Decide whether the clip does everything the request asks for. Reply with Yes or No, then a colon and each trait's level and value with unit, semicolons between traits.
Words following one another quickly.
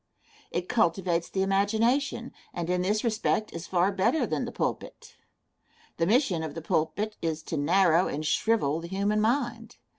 No: average, 160 wpm